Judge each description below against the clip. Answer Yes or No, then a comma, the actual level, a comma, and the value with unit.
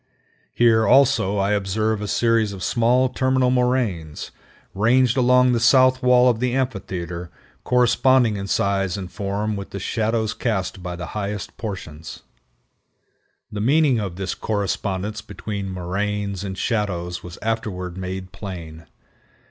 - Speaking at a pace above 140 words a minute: No, slow, 135 wpm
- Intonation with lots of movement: No, average, 4.1 semitones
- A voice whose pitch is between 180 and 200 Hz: No, low, 105 Hz